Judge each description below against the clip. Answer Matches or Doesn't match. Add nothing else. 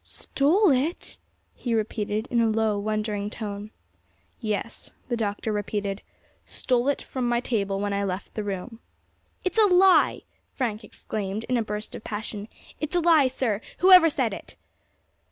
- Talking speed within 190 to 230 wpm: Doesn't match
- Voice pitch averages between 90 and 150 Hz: Doesn't match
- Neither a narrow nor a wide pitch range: Matches